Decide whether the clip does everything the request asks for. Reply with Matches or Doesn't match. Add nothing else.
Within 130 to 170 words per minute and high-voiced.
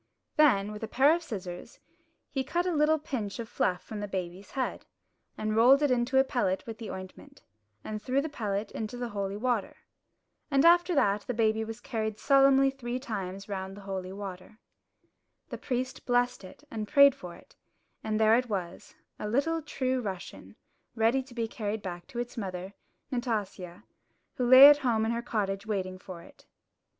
Doesn't match